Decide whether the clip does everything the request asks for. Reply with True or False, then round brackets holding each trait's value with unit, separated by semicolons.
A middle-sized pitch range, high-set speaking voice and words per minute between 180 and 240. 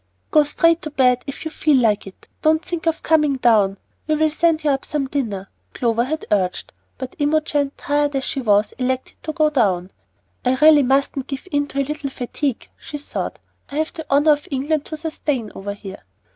True (3.5 semitones; 280 Hz; 200 wpm)